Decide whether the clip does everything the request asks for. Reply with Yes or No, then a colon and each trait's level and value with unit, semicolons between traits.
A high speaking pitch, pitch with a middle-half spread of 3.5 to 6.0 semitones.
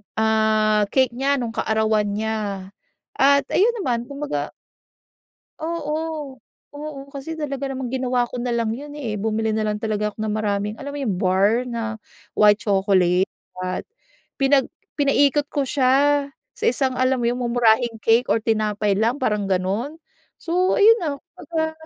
Yes: high, 235 Hz; average, 4.6 semitones